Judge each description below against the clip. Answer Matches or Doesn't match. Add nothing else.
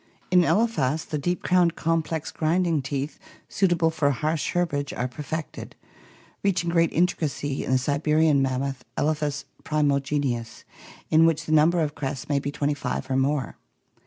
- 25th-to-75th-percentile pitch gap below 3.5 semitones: Matches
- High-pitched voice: Doesn't match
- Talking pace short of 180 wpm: Matches